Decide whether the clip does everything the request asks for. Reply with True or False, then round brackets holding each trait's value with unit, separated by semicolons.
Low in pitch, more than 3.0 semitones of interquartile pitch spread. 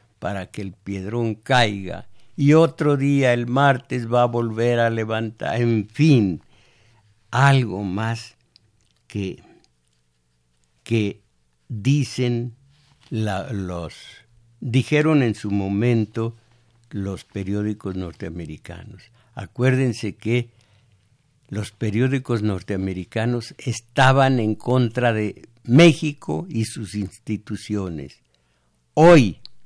True (115 Hz; 3.6 semitones)